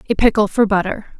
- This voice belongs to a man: No, female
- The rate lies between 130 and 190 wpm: No, average, 200 wpm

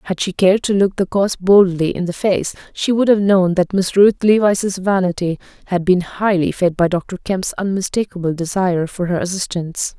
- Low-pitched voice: No, medium, 185 Hz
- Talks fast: No, average, 190 wpm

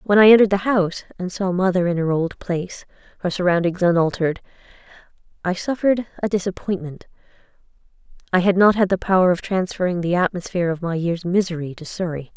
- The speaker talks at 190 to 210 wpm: No, average, 170 wpm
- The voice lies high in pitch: No, medium, 180 Hz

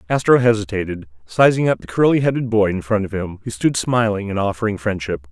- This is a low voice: Yes, low, 105 Hz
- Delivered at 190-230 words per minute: Yes, fast, 205 wpm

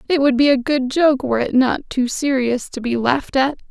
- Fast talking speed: Yes, fast, 245 wpm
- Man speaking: No, female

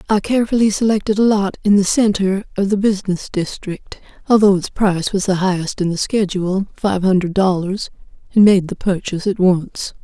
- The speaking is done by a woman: Yes, female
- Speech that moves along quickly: No, average, 165 wpm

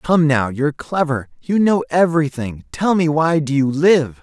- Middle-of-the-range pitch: Yes, medium, 150 Hz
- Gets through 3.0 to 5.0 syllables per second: Yes, 4.6 syllables/s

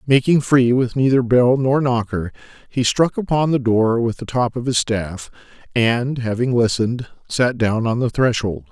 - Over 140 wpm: Yes, average, 180 wpm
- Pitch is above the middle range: No, low, 120 Hz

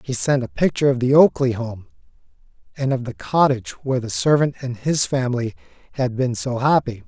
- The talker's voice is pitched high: No, low, 130 Hz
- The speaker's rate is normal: Yes, average, 185 wpm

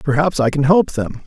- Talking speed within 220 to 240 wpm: Yes, fast, 235 wpm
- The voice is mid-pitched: Yes, medium, 150 Hz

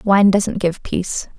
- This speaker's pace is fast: No, average, 175 wpm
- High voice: Yes, high, 195 Hz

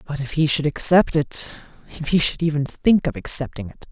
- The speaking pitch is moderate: Yes, medium, 150 Hz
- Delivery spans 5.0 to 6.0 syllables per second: Yes, 5.3 syllables/s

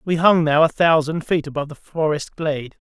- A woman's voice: No, male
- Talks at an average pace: No, fast, 210 wpm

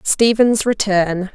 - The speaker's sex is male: No, female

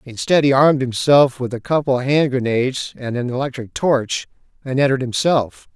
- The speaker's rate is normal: Yes, average, 175 wpm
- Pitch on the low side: Yes, low, 130 Hz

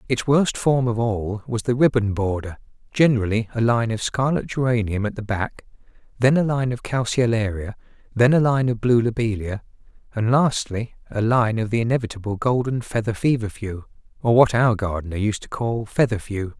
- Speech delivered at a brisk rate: No, average, 170 wpm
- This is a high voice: No, low, 115 Hz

